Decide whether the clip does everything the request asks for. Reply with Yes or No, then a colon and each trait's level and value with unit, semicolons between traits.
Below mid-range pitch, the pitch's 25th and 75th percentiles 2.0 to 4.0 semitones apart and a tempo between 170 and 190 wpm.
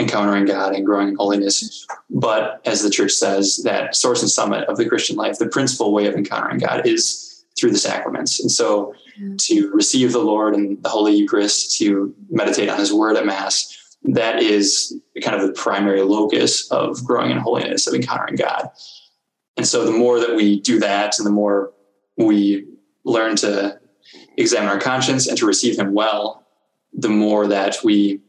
Yes: low, 105 Hz; average, 3.5 semitones; average, 180 wpm